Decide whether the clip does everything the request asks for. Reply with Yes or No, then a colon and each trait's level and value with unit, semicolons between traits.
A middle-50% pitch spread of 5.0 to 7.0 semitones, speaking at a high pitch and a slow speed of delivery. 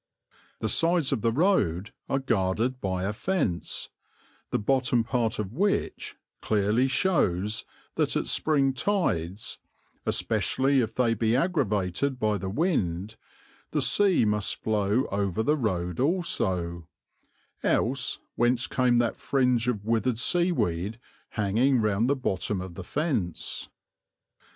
No: wide, 5.5 semitones; low, 115 Hz; slow, 125 wpm